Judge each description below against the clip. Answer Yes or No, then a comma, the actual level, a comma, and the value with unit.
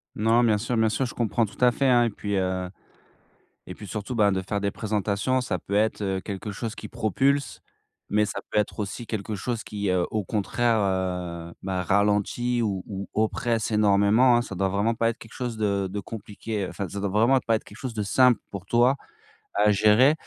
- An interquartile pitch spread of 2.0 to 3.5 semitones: Yes, average, 2.8 semitones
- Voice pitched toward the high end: No, low, 105 Hz